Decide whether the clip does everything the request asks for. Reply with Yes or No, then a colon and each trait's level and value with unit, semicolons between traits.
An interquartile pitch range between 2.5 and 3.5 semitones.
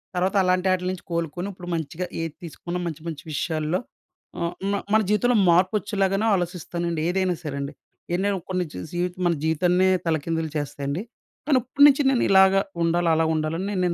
Yes: average, 2.8 semitones